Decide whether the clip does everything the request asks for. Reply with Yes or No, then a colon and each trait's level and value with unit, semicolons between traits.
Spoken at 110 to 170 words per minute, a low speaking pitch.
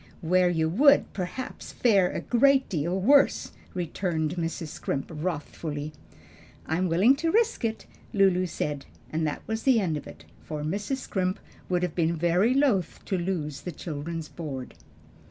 No: average, 160 wpm; medium, 175 Hz